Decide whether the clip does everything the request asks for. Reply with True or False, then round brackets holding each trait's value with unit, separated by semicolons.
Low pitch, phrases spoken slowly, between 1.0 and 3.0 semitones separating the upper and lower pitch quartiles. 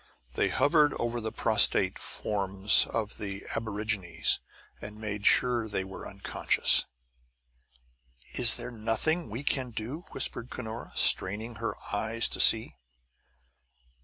True (110 Hz; 125 wpm; 2.6 semitones)